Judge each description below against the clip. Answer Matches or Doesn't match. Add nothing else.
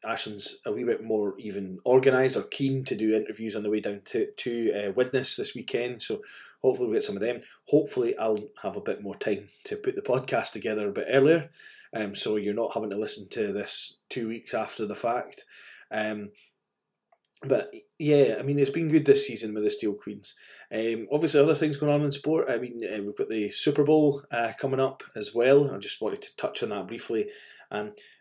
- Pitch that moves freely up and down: Matches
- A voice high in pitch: Doesn't match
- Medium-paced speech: Doesn't match